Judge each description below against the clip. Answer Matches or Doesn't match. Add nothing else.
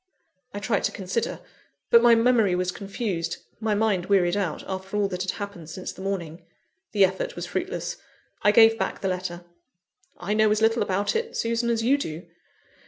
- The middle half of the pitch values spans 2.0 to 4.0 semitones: Matches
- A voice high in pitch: Matches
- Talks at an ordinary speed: Matches